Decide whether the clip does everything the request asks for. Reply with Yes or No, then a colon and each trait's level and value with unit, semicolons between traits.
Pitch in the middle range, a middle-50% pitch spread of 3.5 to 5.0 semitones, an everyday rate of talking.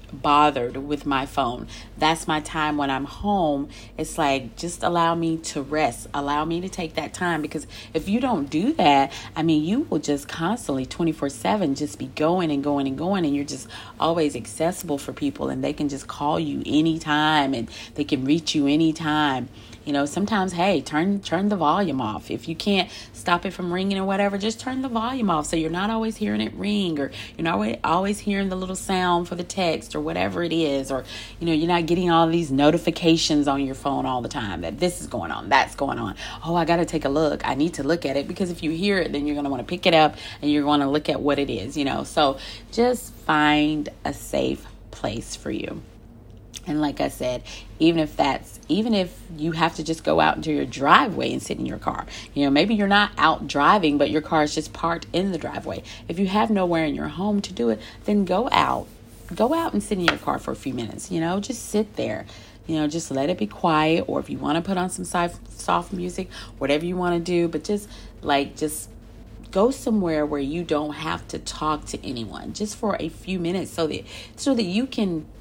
No: medium, 155 Hz; average, 4.4 semitones; fast, 235 wpm